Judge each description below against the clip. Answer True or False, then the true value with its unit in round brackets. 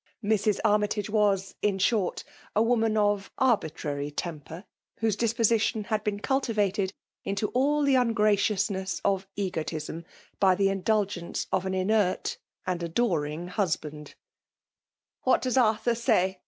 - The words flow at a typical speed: False (130 wpm)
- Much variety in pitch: False (3.0 semitones)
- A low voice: False (205 Hz)